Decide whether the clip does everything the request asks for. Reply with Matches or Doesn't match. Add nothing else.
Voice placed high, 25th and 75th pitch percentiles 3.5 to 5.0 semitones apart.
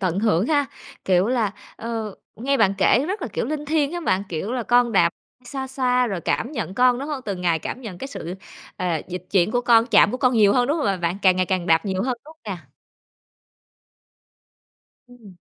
Doesn't match